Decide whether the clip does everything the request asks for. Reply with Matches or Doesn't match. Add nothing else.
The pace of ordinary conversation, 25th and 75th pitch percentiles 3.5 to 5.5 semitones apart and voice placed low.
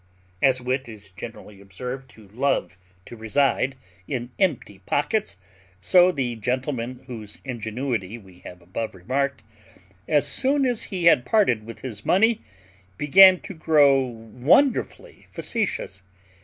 Doesn't match